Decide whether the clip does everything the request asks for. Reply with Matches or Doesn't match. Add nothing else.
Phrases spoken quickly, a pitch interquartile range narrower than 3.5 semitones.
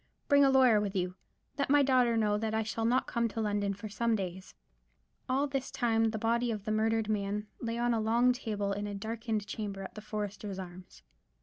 Matches